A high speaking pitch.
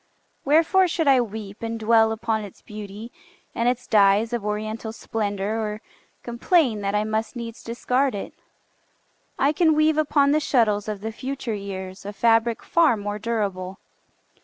Yes: high, 225 Hz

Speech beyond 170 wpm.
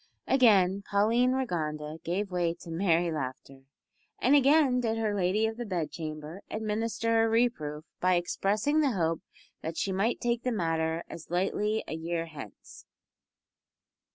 No: average, 145 wpm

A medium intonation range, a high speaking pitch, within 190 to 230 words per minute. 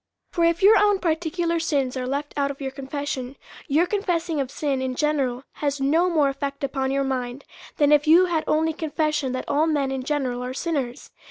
Yes: average, 3.3 semitones; very high, 290 Hz; average, 200 wpm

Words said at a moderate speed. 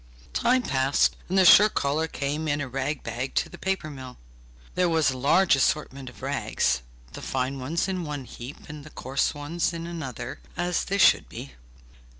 Yes: average, 185 wpm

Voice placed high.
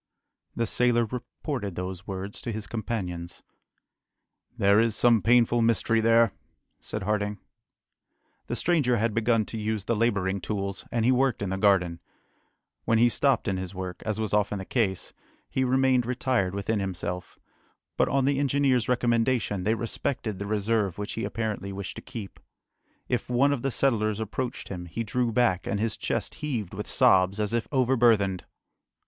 No: low, 110 Hz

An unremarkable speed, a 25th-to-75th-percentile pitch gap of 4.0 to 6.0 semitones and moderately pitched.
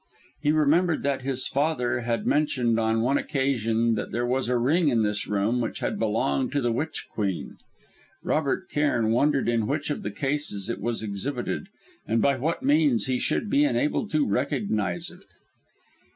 No: average, 175 wpm; average, 4.4 semitones; low, 125 Hz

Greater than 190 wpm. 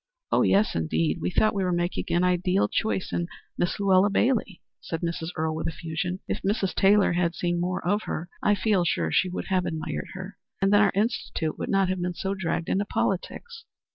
Yes: average, 200 wpm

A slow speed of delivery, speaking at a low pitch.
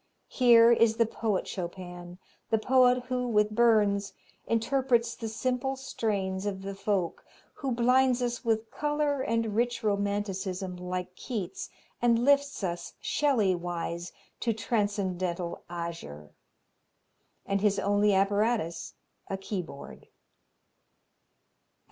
No: slow, 110 wpm; high, 210 Hz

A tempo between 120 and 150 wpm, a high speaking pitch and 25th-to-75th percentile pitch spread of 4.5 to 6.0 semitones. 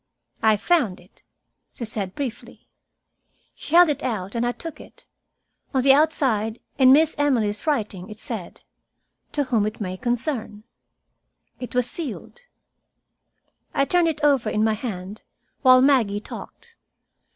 Yes: average, 140 wpm; high, 240 Hz; average, 5.1 semitones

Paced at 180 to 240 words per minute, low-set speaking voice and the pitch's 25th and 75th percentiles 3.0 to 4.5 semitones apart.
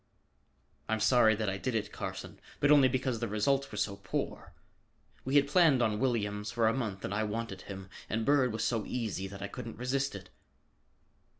Yes: average, 195 wpm; low, 115 Hz; average, 4.0 semitones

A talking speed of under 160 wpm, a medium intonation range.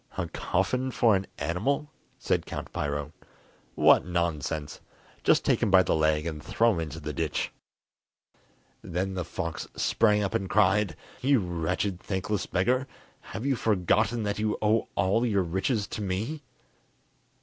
Yes: average, 150 wpm; average, 4.5 semitones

